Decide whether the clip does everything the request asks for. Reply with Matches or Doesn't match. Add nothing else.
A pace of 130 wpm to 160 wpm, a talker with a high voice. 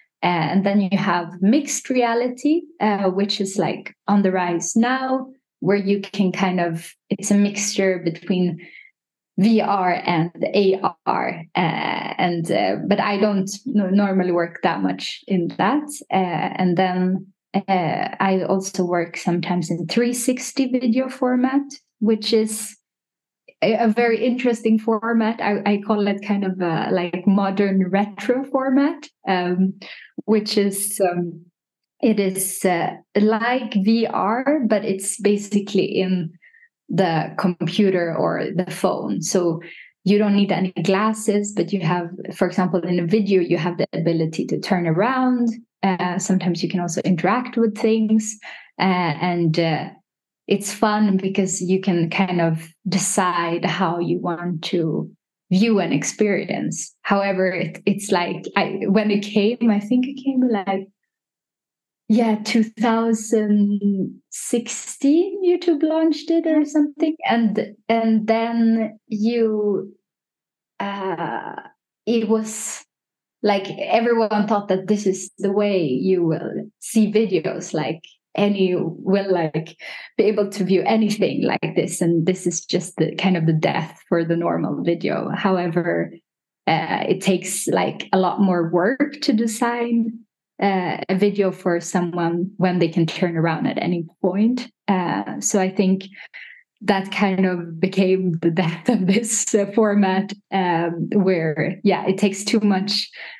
Matches